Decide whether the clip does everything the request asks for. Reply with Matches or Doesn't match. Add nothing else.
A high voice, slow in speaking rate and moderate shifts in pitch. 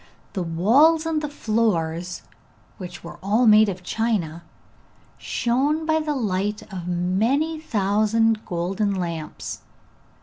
Doesn't match